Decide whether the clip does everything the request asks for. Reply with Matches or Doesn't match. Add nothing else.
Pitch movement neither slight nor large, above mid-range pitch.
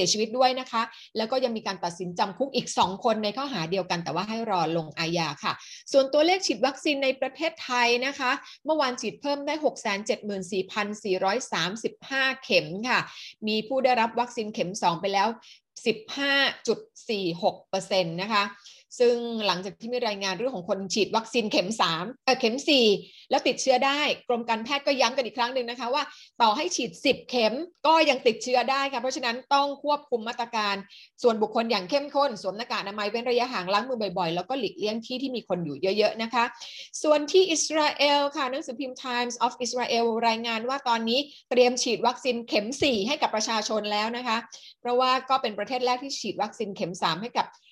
Matches